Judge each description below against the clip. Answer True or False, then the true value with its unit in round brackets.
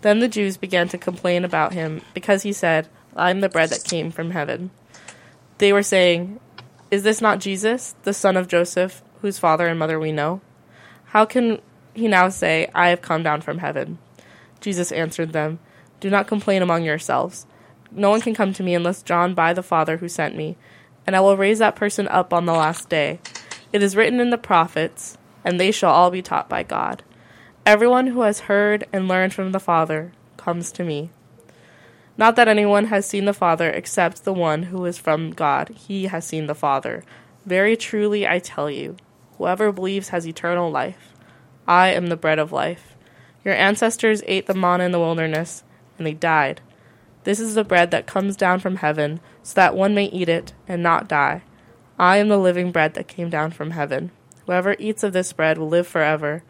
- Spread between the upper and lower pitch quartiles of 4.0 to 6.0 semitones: False (3.6 semitones)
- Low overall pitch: False (180 Hz)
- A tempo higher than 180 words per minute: True (200 wpm)